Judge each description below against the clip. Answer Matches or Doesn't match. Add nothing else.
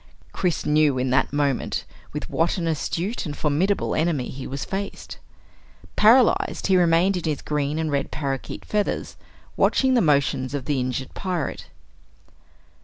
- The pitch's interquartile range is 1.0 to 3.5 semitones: Doesn't match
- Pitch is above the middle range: Doesn't match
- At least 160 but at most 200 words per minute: Doesn't match